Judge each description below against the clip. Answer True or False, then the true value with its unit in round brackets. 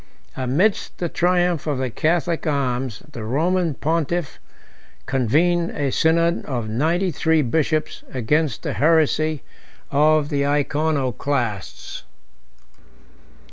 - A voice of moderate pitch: True (150 Hz)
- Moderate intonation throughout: True (3.9 semitones)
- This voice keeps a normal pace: False (100 wpm)